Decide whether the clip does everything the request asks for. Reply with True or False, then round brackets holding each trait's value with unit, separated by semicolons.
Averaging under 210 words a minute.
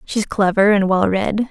True (200 wpm)